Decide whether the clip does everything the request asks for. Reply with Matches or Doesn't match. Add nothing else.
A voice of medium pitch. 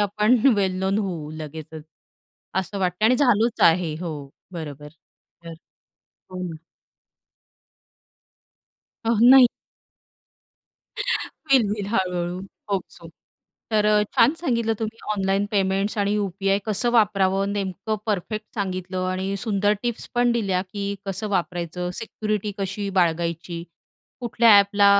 Doesn't match